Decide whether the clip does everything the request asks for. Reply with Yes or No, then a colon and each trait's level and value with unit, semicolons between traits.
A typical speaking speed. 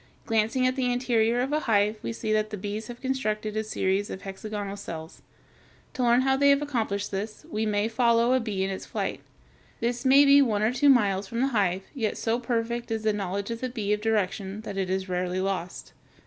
No: fast, 220 wpm